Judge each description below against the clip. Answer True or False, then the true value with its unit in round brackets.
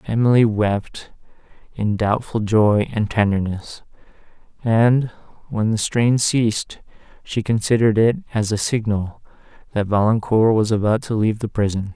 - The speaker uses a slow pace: True (130 wpm)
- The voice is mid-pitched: False (110 Hz)